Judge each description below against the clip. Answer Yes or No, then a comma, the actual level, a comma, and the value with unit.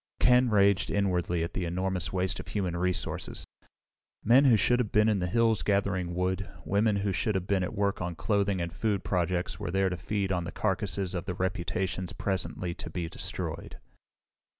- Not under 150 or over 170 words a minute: No, average, 190 wpm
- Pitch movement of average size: No, narrow, 2.3 semitones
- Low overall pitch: Yes, very low, 95 Hz